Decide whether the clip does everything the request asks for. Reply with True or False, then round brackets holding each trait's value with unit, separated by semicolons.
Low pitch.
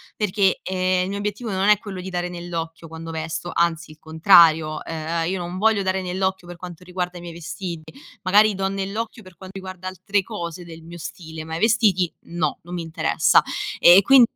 False (180 Hz)